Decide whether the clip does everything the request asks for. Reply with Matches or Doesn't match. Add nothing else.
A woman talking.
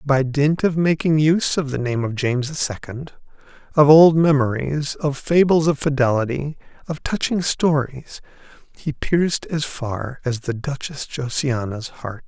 Doesn't match